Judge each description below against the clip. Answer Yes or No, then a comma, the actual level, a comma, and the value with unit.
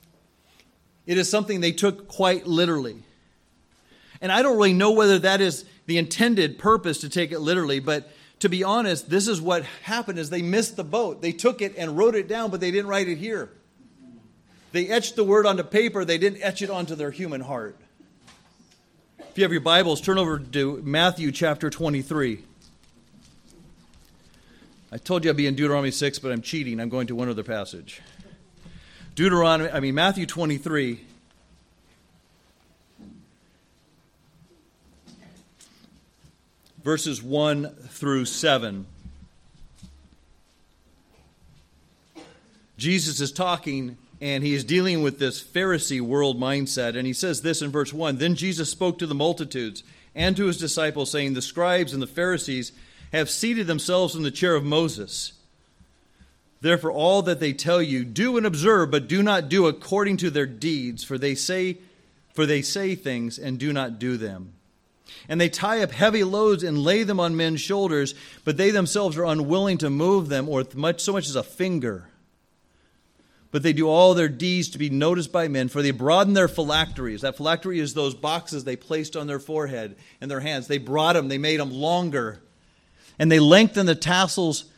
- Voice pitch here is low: No, medium, 160 Hz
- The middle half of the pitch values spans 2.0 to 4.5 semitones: No, average, 5.1 semitones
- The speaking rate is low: No, average, 170 wpm